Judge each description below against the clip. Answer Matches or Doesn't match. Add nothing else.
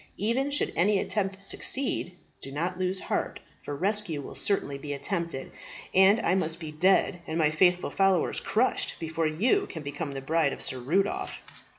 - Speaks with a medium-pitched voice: Matches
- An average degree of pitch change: Matches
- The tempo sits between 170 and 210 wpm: Matches